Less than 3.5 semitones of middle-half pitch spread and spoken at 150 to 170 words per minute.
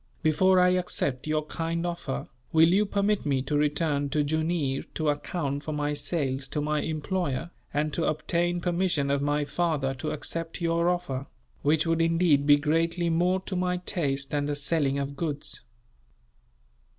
Yes: average, 3.0 semitones; average, 165 wpm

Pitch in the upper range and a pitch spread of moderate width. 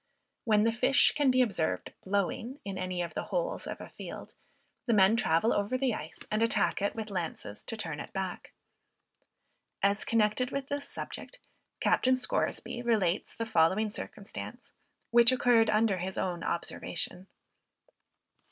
Yes: high, 215 Hz; average, 4.3 semitones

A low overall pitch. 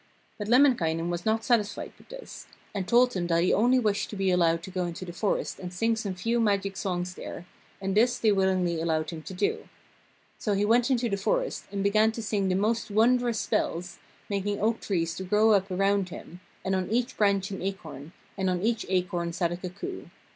No: high, 195 Hz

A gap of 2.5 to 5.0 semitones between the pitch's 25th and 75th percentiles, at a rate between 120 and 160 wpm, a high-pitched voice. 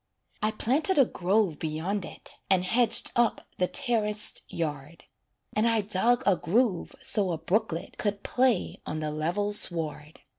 No: wide, 5.4 semitones; average, 150 wpm; high, 205 Hz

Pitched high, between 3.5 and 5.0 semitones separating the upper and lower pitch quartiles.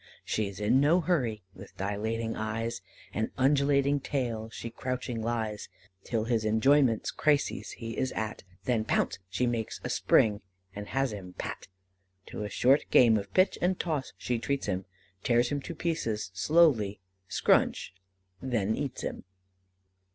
No: low, 115 Hz; average, 4.2 semitones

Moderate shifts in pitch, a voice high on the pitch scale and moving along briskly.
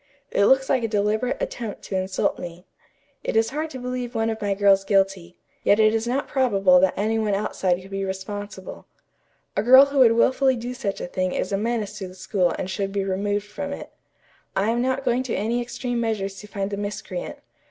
Yes: average, 3.8 semitones; high, 210 Hz; fast, 215 wpm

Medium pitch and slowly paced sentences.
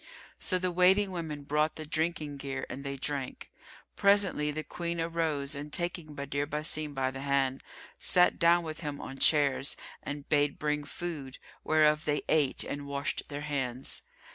No: medium, 150 Hz; average, 165 wpm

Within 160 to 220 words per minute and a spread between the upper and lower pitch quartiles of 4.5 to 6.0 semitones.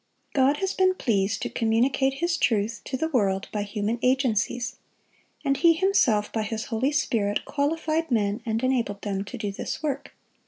Yes: average, 170 wpm; average, 5.3 semitones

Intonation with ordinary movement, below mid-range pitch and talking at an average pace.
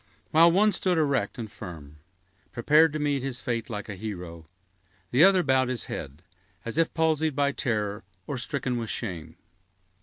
No: wide, 6.7 semitones; low, 125 Hz; average, 170 wpm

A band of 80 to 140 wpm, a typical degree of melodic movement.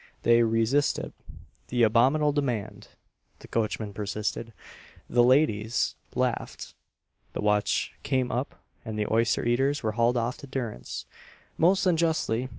Yes: slow, 135 wpm; average, 3.5 semitones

